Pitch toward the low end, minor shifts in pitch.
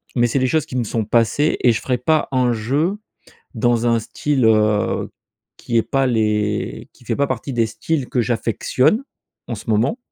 No: low, 120 Hz; average, 3.3 semitones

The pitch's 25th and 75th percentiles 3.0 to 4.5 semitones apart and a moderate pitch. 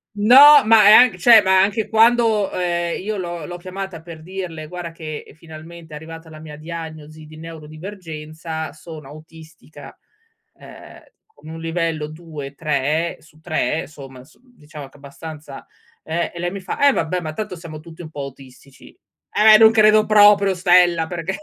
Yes: average, 3.5 semitones; medium, 165 Hz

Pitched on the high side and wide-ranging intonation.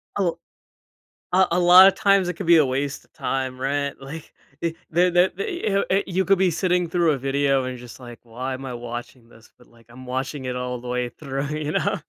No: medium, 140 Hz; wide, 5.8 semitones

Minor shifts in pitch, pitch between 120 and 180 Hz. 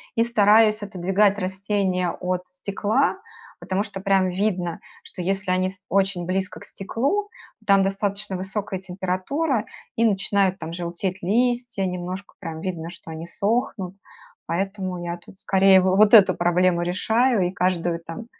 No: narrow, 2.3 semitones; high, 190 Hz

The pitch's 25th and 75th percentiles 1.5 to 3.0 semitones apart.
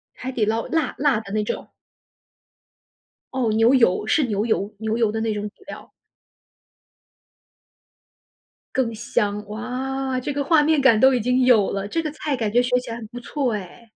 No: average, 3.5 semitones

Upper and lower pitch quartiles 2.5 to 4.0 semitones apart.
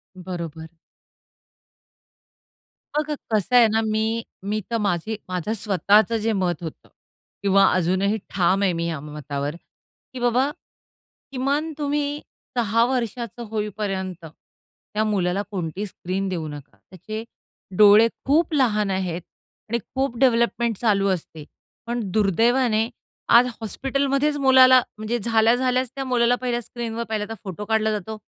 No: average, 4.4 semitones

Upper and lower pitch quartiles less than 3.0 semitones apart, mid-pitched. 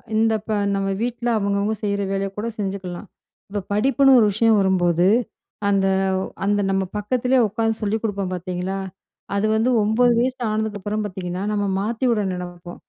No: narrow, 2.6 semitones; high, 205 Hz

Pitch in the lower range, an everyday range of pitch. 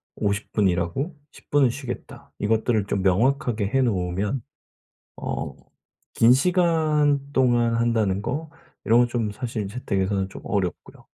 Yes: low, 115 Hz; average, 4.9 semitones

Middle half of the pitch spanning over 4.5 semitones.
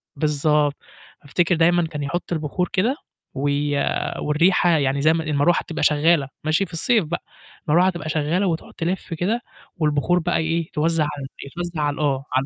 No: average, 2.9 semitones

